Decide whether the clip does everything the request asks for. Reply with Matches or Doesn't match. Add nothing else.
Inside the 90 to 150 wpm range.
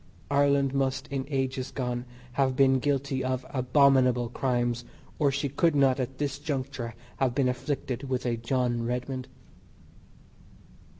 Matches